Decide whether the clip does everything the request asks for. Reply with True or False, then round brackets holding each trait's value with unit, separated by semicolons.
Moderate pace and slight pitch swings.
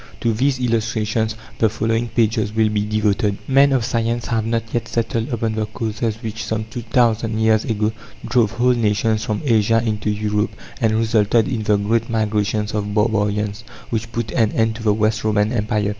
True (185 wpm; 1.4 semitones)